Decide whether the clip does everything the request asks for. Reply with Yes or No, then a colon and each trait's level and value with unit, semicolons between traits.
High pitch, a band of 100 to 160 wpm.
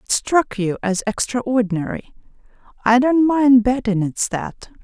Yes: high, 235 Hz; slow, 135 wpm